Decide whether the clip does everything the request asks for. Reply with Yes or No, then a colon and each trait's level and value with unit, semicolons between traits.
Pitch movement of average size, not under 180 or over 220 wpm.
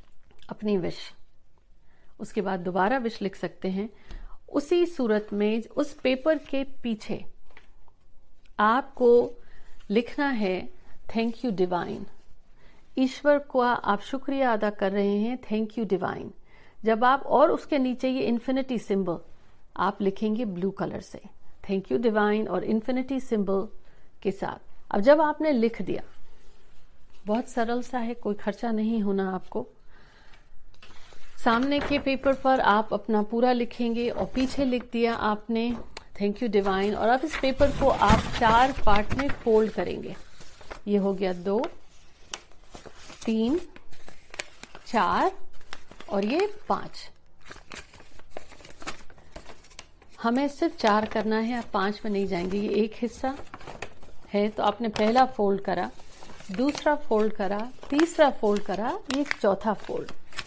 No: average, 4.3 semitones; average, 130 wpm